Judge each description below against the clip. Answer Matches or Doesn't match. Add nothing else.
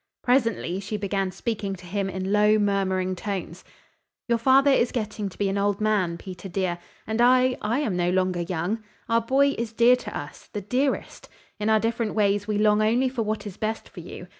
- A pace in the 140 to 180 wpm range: Doesn't match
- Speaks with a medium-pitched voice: Doesn't match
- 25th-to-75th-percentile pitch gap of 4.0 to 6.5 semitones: Doesn't match